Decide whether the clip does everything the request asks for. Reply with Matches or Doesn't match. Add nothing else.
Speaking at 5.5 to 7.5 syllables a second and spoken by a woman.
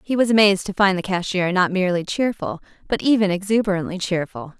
Matches